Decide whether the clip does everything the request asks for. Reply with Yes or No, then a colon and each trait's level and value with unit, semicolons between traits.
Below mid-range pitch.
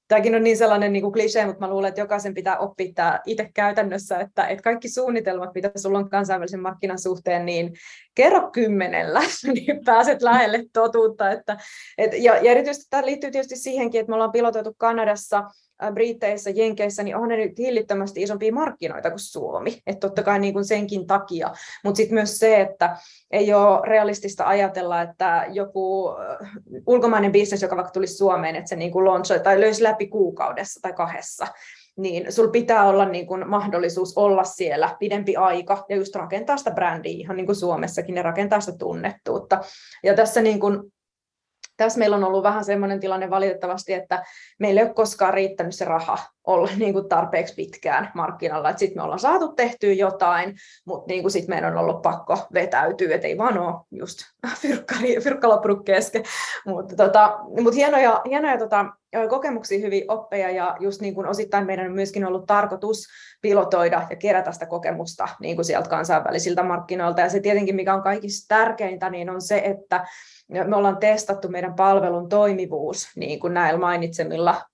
No: high, 200 Hz